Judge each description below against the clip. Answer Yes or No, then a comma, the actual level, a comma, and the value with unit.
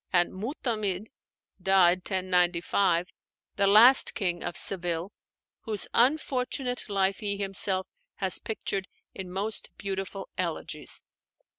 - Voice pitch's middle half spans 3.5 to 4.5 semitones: No, average, 2.7 semitones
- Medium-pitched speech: No, high, 195 Hz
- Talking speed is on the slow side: Yes, slow, 105 wpm